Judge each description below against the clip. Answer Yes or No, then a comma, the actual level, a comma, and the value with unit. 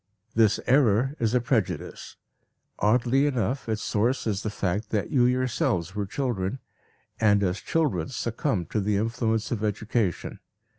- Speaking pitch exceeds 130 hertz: No, low, 110 Hz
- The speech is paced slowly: No, average, 145 wpm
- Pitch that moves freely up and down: No, average, 3.3 semitones